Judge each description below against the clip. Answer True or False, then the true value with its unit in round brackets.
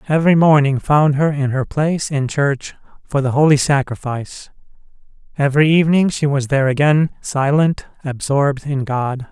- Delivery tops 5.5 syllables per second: False (5.2 syllables/s)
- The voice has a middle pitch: True (145 Hz)